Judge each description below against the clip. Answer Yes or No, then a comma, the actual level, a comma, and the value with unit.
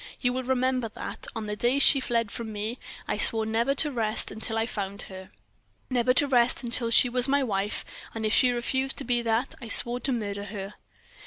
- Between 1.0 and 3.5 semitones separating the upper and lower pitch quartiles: Yes, average, 2.8 semitones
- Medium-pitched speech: No, high, 235 Hz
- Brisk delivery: Yes, fast, 215 wpm